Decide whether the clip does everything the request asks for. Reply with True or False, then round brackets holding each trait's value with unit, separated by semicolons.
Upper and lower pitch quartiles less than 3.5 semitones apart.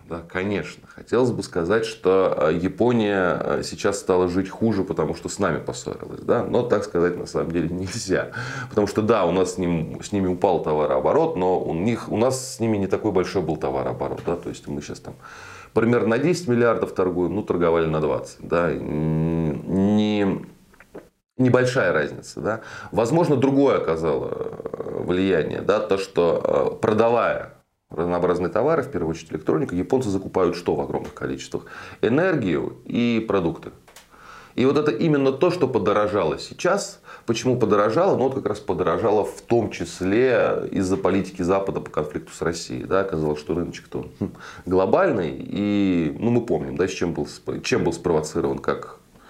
False (5.2 semitones)